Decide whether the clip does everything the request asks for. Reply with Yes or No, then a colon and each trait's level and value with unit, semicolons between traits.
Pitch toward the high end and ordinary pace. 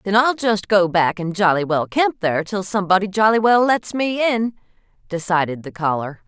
Yes: high, 195 Hz; average, 190 wpm